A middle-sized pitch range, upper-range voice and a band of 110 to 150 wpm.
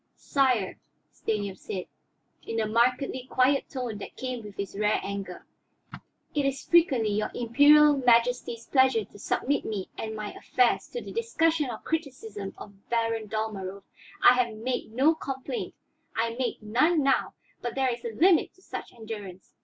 No: average, 4.1 semitones; high, 235 Hz; average, 160 wpm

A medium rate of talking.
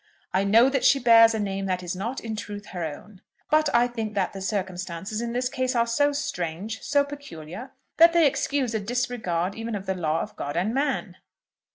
No: fast, 210 wpm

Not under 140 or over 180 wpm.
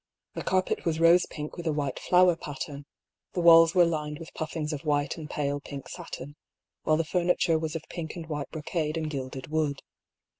No: average, 200 wpm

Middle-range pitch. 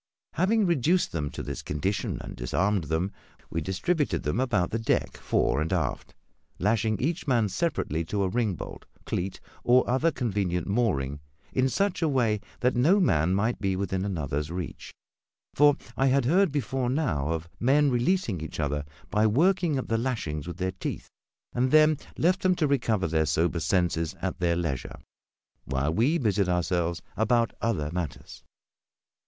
No: low, 105 Hz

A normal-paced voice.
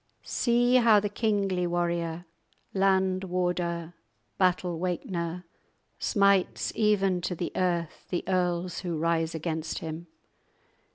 No: slow, 115 wpm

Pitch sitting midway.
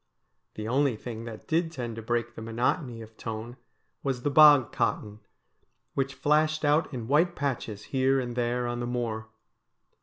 No: low, 120 Hz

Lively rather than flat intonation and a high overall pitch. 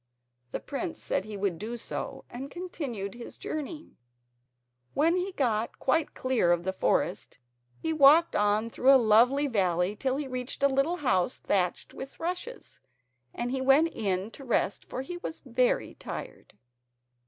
Yes: wide, 6.4 semitones; very high, 260 Hz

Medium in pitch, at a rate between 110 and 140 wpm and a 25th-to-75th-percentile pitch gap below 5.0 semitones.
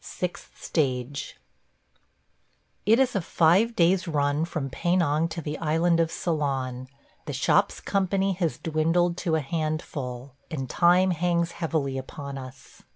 Yes: medium, 160 Hz; slow, 135 wpm; average, 3.7 semitones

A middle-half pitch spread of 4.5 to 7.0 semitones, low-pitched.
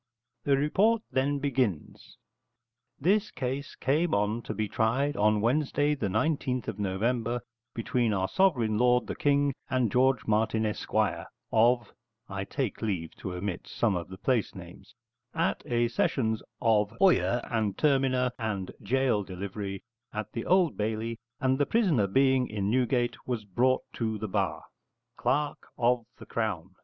No: average, 4.1 semitones; low, 120 Hz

